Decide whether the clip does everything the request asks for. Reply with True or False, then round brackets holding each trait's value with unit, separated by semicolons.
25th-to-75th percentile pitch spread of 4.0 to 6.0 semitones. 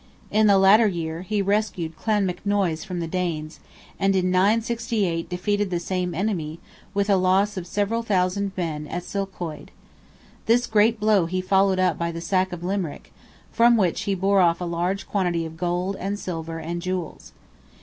False (2.9 semitones)